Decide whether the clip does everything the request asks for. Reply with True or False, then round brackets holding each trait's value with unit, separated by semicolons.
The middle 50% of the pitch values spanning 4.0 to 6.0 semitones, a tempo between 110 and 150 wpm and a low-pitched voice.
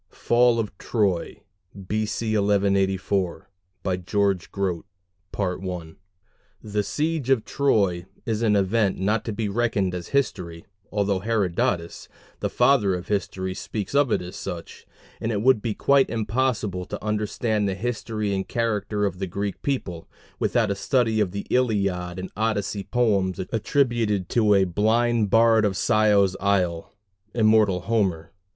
False (3.1 semitones; 140 wpm; 105 Hz)